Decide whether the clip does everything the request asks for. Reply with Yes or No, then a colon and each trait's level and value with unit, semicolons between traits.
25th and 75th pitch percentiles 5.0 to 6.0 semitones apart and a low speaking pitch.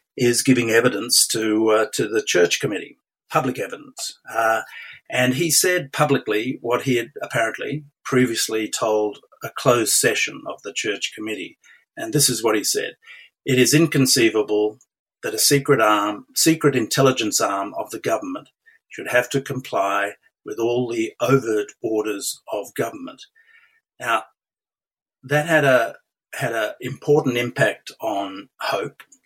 Yes: wide, 5.5 semitones; low, 130 Hz